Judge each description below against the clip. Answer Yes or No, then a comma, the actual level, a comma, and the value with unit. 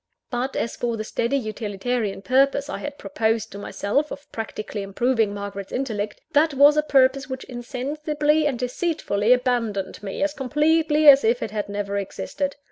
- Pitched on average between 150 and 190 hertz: No, very high, 250 Hz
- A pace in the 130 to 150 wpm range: No, average, 165 wpm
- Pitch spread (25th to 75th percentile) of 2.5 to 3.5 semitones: No, average, 5.2 semitones